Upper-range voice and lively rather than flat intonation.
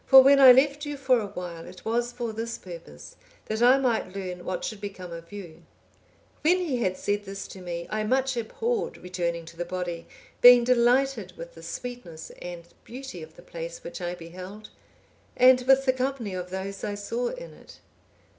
Yes: high, 215 Hz; wide, 6.2 semitones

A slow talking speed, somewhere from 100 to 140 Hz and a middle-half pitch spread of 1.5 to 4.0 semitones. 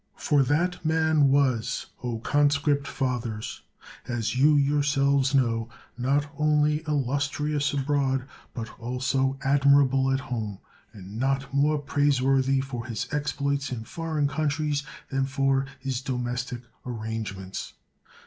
Yes: slow, 120 wpm; low, 135 Hz; narrow, 2.6 semitones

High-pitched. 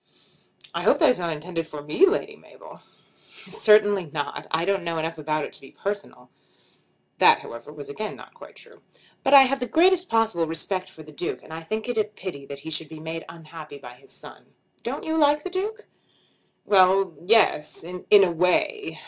No: medium, 180 Hz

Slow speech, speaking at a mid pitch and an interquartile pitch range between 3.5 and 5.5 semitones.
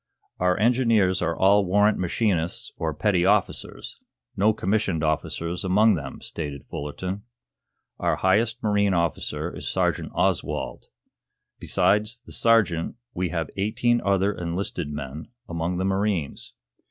No: slow, 125 wpm; very low, 95 Hz; average, 3.8 semitones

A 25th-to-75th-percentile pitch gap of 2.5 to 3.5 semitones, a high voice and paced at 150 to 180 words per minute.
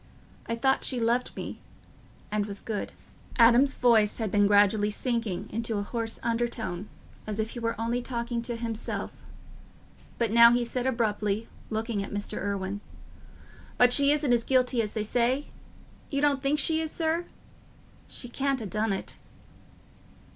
Yes: average, 2.9 semitones; high, 230 Hz; average, 160 wpm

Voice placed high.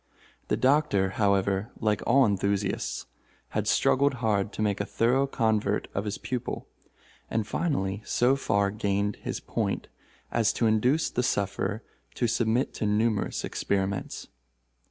No: low, 110 Hz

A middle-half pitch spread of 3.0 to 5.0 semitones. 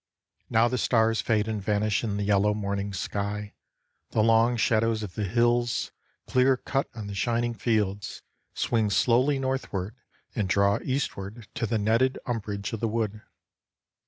No: narrow, 2.6 semitones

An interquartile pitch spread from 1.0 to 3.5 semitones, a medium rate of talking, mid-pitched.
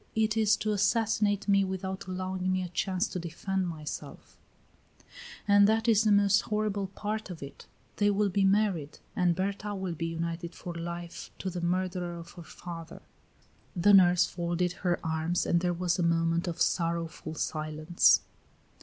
Yes: average, 2.9 semitones; average, 165 wpm; medium, 180 Hz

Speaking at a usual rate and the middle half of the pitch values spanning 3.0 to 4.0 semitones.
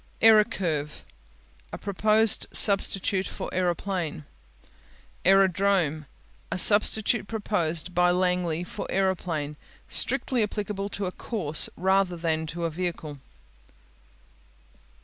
No: slow, 95 wpm; average, 3.3 semitones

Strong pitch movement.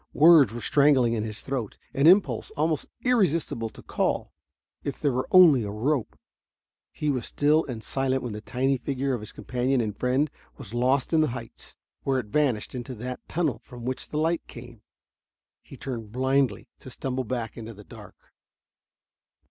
No: average, 3.6 semitones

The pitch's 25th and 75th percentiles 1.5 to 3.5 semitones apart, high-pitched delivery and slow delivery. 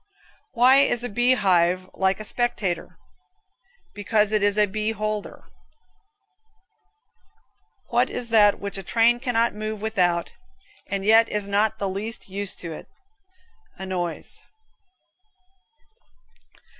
Yes: average, 2.7 semitones; high, 210 Hz; slow, 120 wpm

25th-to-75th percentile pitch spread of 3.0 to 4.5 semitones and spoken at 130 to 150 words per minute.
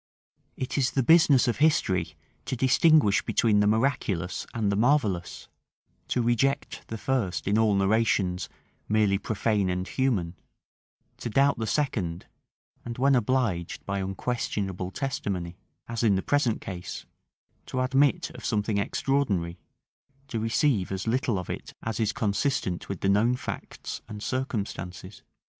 No: average, 4.9 semitones; average, 140 wpm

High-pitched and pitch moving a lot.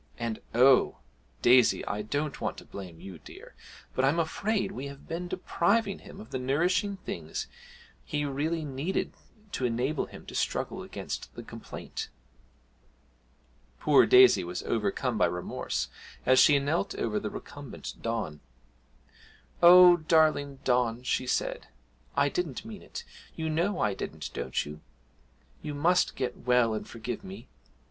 No: medium, 140 Hz; wide, 6.3 semitones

